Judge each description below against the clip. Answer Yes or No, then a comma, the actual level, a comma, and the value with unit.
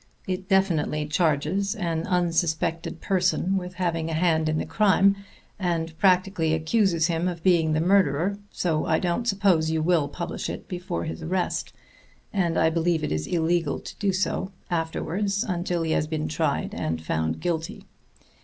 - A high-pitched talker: No, medium, 170 Hz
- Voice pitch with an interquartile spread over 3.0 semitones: No, average, 2.7 semitones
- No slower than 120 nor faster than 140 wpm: No, average, 165 wpm